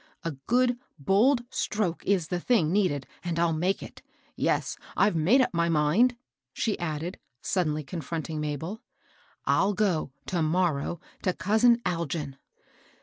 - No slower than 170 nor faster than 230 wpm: No, average, 145 wpm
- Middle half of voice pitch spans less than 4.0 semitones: No, average, 4.9 semitones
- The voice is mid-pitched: Yes, medium, 175 Hz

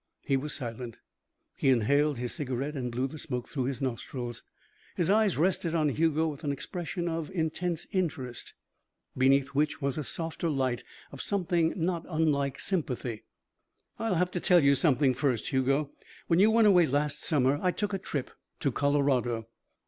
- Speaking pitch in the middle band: Yes, medium, 145 Hz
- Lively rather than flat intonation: No, average, 4.2 semitones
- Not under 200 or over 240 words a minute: No, average, 170 wpm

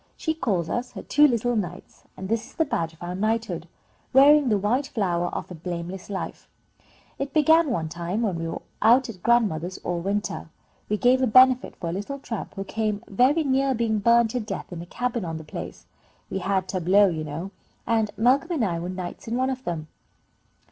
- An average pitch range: No, wide, 5.9 semitones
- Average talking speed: No, fast, 210 wpm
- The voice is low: No, high, 210 Hz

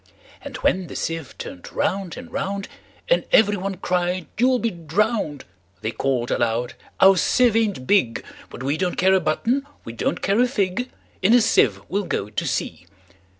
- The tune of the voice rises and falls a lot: Yes, wide, 8.3 semitones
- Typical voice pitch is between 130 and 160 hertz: No, medium, 185 Hz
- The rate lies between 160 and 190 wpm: Yes, average, 170 wpm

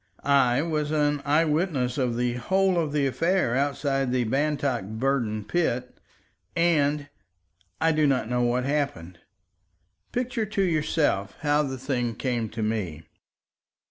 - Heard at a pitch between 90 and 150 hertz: Yes, low, 135 Hz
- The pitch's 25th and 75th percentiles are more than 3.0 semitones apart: Yes, average, 4.1 semitones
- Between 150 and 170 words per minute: No, slow, 135 wpm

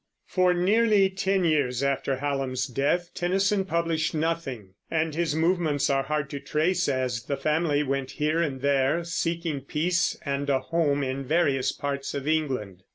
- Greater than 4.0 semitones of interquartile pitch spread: No, average, 3.7 semitones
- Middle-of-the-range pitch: Yes, medium, 150 Hz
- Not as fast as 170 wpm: Yes, average, 160 wpm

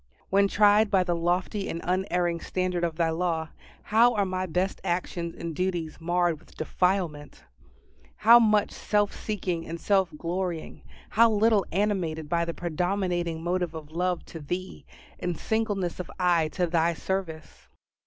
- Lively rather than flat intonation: No, narrow, 2.6 semitones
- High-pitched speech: No, medium, 180 Hz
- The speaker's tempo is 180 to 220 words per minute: No, average, 155 wpm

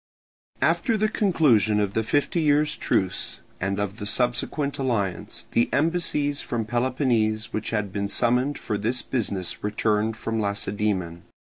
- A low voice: Yes, low, 110 Hz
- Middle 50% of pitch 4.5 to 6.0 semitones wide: Yes, average, 5.2 semitones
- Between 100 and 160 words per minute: Yes, average, 140 wpm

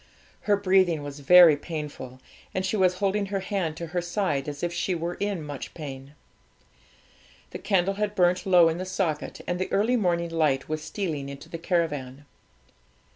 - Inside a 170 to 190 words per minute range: Yes, average, 180 wpm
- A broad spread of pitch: No, average, 4.1 semitones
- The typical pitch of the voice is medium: Yes, medium, 175 Hz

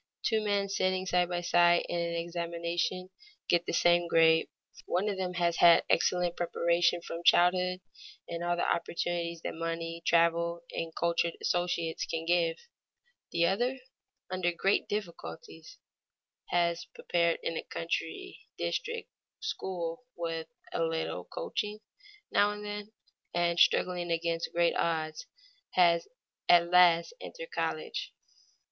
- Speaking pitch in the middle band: Yes, medium, 175 Hz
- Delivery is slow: Yes, slow, 130 wpm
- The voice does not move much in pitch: Yes, narrow, 1.5 semitones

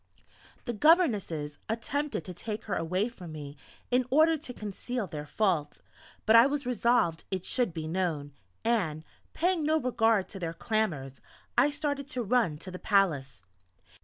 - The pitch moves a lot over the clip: Yes, wide, 7.4 semitones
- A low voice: No, high, 210 Hz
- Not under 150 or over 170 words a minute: Yes, average, 160 wpm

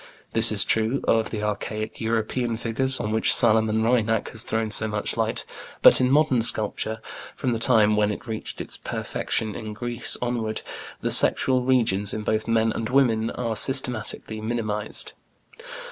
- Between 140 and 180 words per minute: Yes, average, 160 wpm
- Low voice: Yes, low, 110 Hz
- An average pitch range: No, narrow, 1.8 semitones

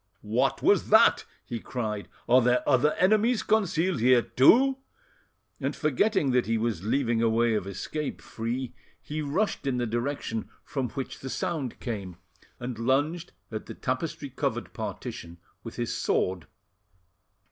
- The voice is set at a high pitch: No, low, 125 Hz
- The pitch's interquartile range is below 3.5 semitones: No, average, 5.0 semitones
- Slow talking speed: No, average, 145 wpm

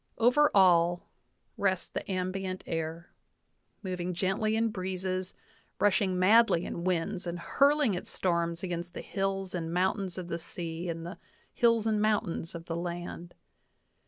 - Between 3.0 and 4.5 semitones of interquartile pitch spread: No, narrow, 2.5 semitones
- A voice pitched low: No, medium, 185 Hz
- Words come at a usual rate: Yes, average, 145 wpm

